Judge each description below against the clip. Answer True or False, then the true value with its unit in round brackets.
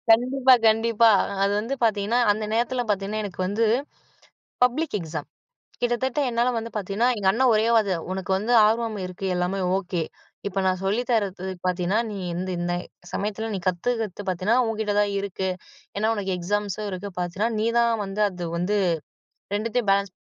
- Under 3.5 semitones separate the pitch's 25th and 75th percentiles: True (3.1 semitones)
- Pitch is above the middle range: True (205 Hz)